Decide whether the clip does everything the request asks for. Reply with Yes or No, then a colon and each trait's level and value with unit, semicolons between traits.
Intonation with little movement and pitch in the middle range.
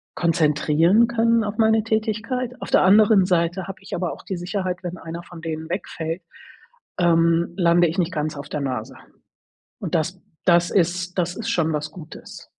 No: average, 3.2 semitones; medium, 175 Hz